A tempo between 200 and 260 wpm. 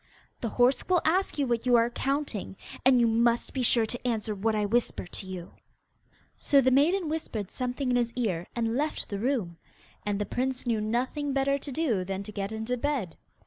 Yes: fast, 205 wpm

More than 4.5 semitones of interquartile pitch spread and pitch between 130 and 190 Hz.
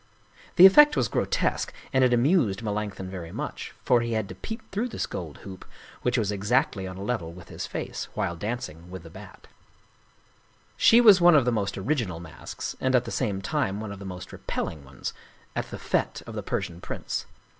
No: wide, 5.6 semitones; low, 105 Hz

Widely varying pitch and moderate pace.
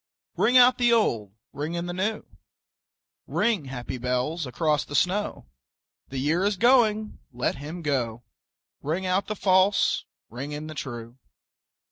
Yes: wide, 7.4 semitones; average, 145 wpm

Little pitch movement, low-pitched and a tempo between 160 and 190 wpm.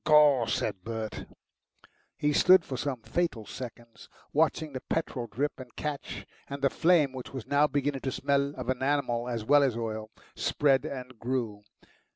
No: average, 3.6 semitones; low, 130 Hz; average, 165 wpm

